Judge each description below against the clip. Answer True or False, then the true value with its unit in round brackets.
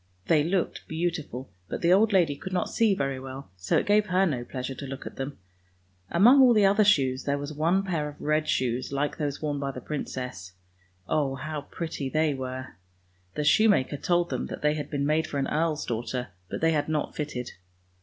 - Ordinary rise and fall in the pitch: True (4.2 semitones)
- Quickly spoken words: True (210 wpm)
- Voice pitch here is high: False (150 Hz)